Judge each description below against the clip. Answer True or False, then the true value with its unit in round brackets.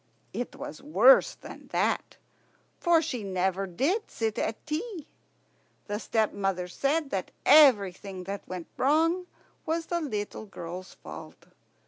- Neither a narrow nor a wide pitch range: False (8.5 semitones)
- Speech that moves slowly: True (125 wpm)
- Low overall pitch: False (220 Hz)